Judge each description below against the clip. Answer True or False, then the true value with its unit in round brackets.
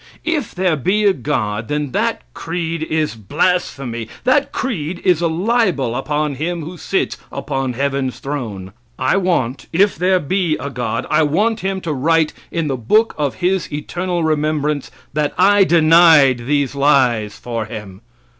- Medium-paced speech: True (155 wpm)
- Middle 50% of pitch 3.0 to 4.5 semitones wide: False (5.0 semitones)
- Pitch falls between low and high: True (155 Hz)